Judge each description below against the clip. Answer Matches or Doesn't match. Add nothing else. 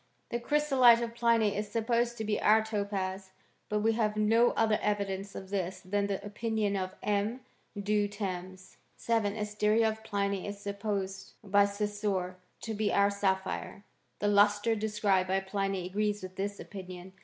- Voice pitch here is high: Matches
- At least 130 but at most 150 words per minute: Doesn't match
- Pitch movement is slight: Matches